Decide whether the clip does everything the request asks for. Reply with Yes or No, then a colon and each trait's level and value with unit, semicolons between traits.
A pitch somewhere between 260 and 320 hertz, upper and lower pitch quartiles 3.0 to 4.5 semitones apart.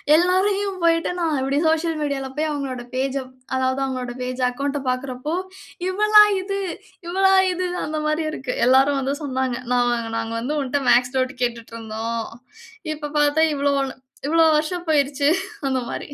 Yes: very high, 280 Hz; average, 3.9 semitones